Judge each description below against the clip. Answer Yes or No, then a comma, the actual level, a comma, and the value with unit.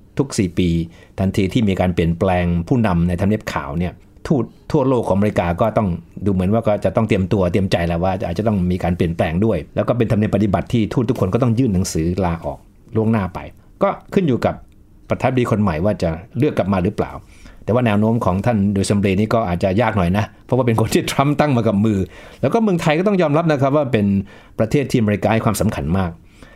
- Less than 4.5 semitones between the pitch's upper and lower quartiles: Yes, average, 4.0 semitones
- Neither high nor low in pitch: No, low, 105 Hz